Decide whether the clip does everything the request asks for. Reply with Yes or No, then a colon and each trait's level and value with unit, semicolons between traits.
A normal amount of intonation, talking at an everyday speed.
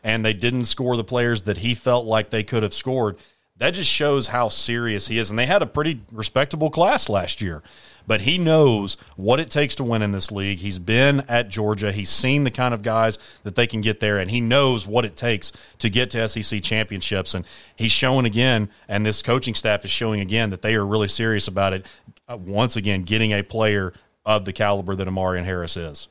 No: average, 3.1 semitones; fast, 225 wpm